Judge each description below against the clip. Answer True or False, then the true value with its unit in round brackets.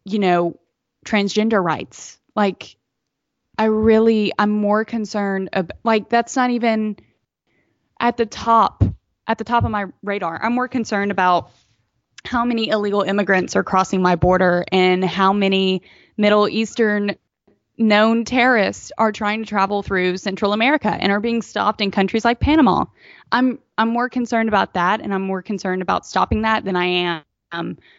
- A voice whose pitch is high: True (205 Hz)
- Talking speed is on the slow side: False (160 wpm)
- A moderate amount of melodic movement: True (3.0 semitones)